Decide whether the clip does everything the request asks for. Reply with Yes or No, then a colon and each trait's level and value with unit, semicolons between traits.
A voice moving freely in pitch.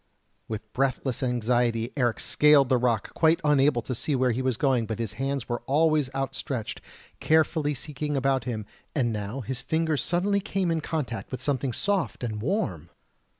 No: average, 4.0 semitones